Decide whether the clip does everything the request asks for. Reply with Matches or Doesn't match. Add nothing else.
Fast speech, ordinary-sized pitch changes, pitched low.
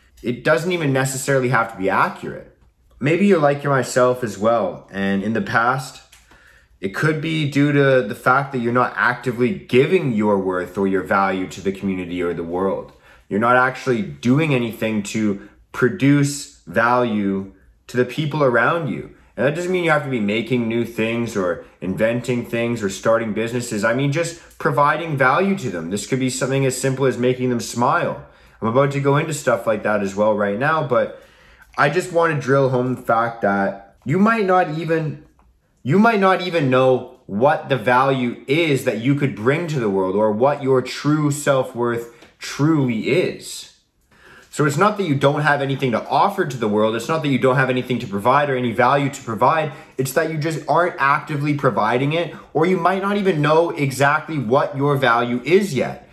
Doesn't match